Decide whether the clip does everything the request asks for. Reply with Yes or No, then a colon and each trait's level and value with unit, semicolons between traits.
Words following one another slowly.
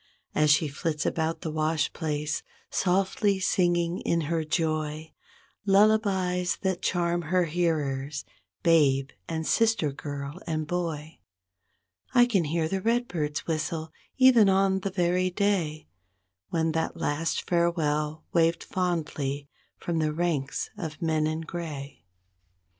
Yes: slow, 125 wpm